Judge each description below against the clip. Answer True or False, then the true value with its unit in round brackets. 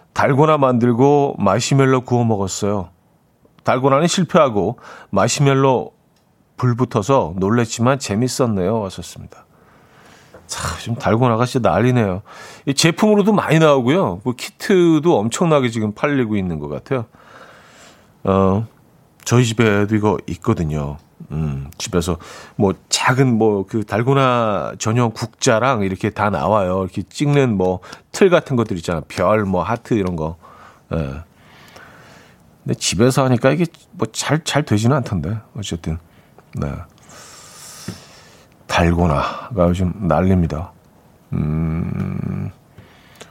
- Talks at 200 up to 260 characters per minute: True (250 characters per minute)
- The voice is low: True (115 Hz)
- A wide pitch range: True (6.4 semitones)